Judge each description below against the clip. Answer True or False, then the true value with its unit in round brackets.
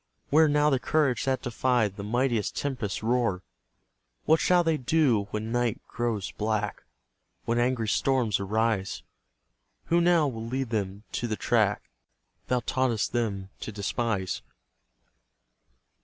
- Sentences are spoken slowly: True (130 wpm)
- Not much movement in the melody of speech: False (3.8 semitones)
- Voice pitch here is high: False (120 Hz)